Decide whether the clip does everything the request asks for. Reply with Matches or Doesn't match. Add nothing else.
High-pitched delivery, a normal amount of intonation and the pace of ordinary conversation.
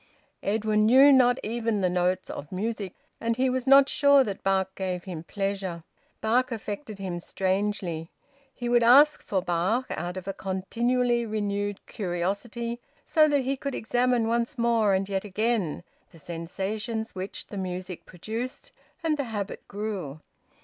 Matches